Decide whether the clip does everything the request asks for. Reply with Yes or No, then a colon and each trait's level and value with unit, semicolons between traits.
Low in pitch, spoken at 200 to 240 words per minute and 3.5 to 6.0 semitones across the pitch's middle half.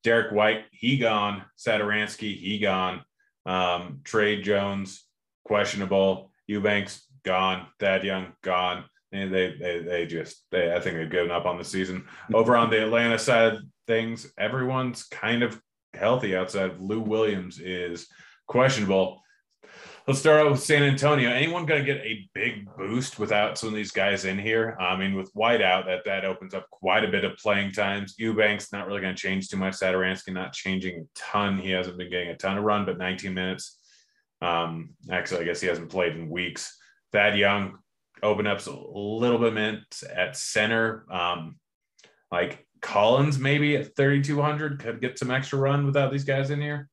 No: low, 105 Hz; average, 180 wpm; average, 3.8 semitones